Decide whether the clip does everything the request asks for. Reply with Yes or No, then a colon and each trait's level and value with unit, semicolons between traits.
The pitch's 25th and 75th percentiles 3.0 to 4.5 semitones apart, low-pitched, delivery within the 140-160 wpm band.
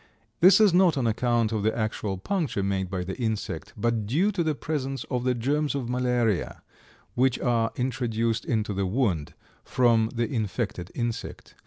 No: average, 3.5 semitones; low, 120 Hz; average, 170 wpm